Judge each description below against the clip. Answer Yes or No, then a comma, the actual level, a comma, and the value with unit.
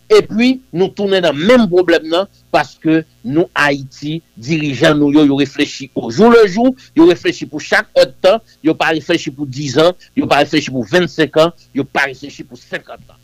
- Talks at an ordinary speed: Yes, average, 200 wpm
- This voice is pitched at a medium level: Yes, medium, 160 Hz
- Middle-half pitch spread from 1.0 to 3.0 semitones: No, average, 4.8 semitones